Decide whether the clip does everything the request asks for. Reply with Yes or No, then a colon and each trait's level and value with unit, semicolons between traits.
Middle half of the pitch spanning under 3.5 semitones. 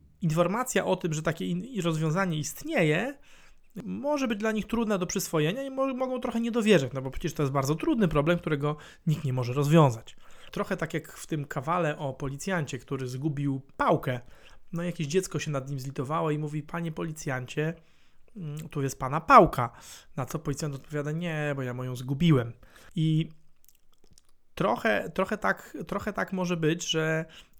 No: average, 3.8 semitones